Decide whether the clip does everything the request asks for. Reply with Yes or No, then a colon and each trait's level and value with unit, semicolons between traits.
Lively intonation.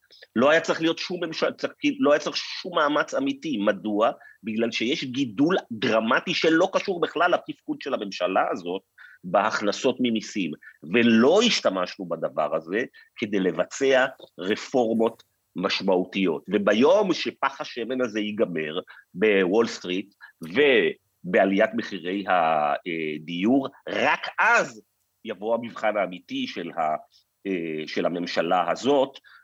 Yes: wide, 9.0 semitones